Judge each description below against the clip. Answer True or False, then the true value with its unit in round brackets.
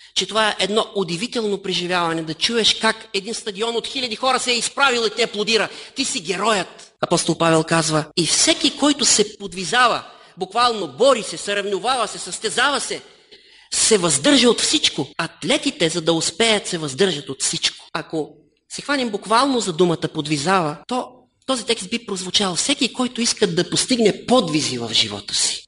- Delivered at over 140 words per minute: True (165 wpm)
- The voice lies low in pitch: False (210 Hz)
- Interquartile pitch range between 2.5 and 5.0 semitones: False (5.6 semitones)